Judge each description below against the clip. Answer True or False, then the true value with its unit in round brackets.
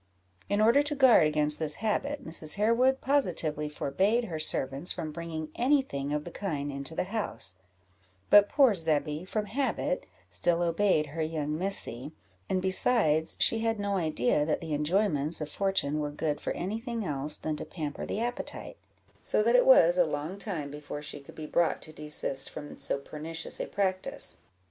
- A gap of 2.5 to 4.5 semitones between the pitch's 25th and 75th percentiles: False (5.5 semitones)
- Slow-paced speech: False (180 wpm)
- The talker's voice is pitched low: False (165 Hz)